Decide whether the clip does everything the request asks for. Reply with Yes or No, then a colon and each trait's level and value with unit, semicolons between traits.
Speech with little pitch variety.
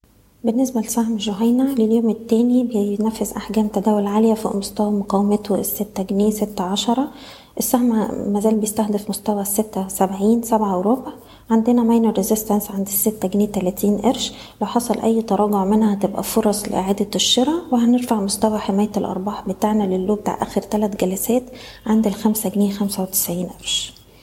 Yes: narrow, 2.1 semitones